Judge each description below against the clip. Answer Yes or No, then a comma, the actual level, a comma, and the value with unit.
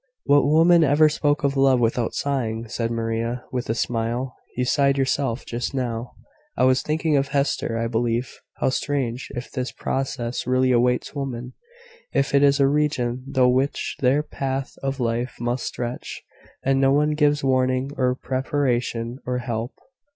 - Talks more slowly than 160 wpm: No, average, 165 wpm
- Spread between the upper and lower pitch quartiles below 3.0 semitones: Yes, narrow, 2.5 semitones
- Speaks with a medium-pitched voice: No, low, 130 Hz